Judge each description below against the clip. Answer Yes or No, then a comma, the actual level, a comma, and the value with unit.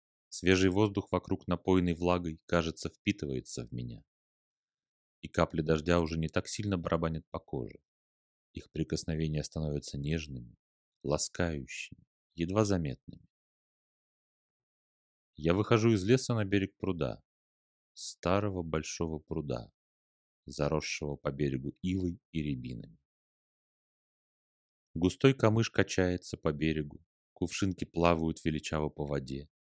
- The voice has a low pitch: Yes, very low, 80 Hz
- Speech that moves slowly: Yes, slow, 105 wpm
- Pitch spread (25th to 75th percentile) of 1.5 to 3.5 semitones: No, average, 4.4 semitones